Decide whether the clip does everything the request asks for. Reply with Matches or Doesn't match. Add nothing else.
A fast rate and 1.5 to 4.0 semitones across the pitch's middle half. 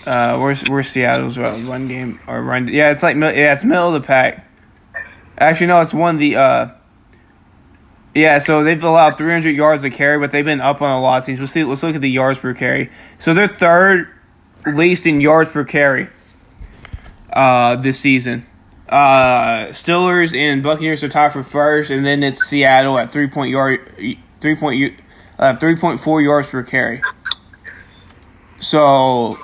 Doesn't match